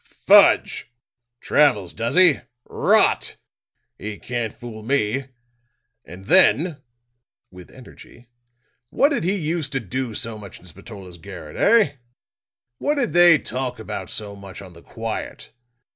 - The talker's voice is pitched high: No, low, 115 Hz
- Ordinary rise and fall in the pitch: No, wide, 7.0 semitones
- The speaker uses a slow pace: Yes, slow, 130 wpm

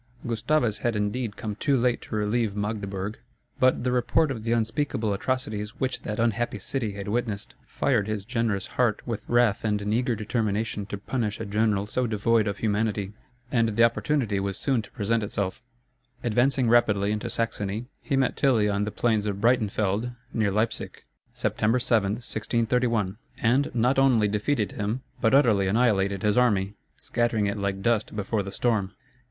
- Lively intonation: No, average, 2.7 semitones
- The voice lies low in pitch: Yes, low, 110 Hz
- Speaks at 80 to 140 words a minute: No, average, 170 wpm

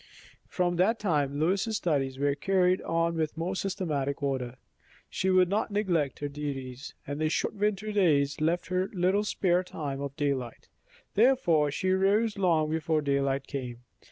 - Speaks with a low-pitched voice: No, medium, 165 Hz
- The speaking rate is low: No, average, 155 wpm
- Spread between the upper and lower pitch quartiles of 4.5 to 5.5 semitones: Yes, average, 5.0 semitones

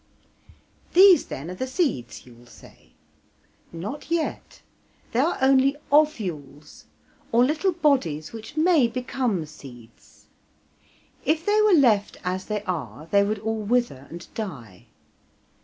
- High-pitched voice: Yes, high, 220 Hz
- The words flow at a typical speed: No, slow, 125 wpm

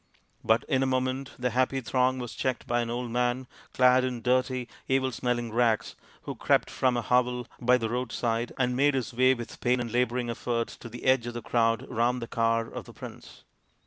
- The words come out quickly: Yes, fast, 210 wpm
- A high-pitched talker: No, low, 125 Hz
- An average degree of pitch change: No, narrow, 1.5 semitones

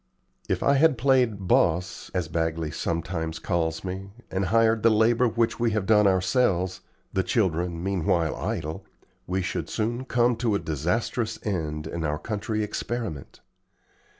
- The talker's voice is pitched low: Yes, very low, 95 Hz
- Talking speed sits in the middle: Yes, average, 150 wpm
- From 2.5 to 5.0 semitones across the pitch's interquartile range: No, wide, 5.4 semitones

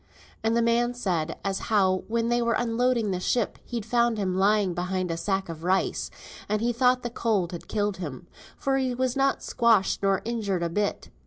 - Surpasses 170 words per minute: Yes, average, 200 wpm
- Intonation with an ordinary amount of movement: Yes, average, 4.1 semitones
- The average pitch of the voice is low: No, high, 215 Hz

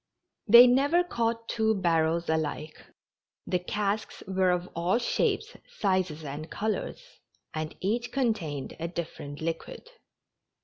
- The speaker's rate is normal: No, slow, 120 wpm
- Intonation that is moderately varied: No, wide, 6.0 semitones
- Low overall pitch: No, medium, 185 Hz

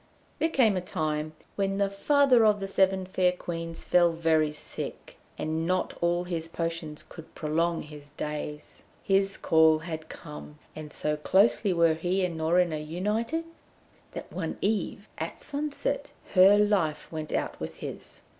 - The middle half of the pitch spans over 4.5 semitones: No, average, 3.7 semitones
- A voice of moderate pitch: Yes, medium, 170 Hz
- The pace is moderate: Yes, average, 155 wpm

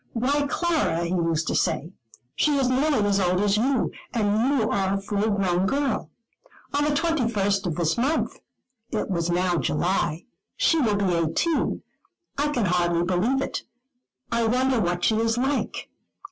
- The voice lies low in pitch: No, high, 210 Hz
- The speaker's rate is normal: Yes, average, 165 wpm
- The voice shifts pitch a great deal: Yes, wide, 6.9 semitones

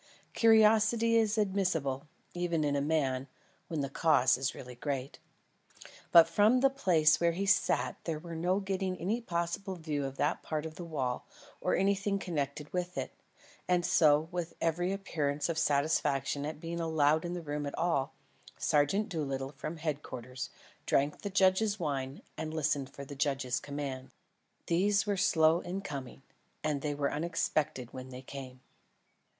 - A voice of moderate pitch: Yes, medium, 160 Hz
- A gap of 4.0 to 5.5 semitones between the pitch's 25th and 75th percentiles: Yes, average, 4.4 semitones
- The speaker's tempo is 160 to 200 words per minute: Yes, average, 165 wpm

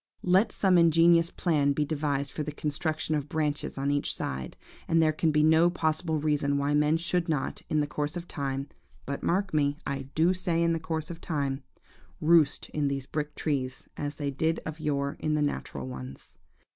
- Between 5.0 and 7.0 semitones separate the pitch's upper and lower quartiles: No, narrow, 2.5 semitones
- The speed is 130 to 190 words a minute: Yes, average, 185 wpm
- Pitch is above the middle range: No, medium, 150 Hz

